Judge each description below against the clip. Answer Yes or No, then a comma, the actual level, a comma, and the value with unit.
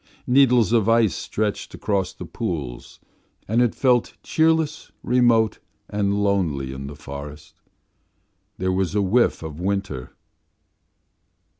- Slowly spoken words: Yes, slow, 120 wpm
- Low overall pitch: Yes, low, 100 Hz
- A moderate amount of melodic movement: No, wide, 6.4 semitones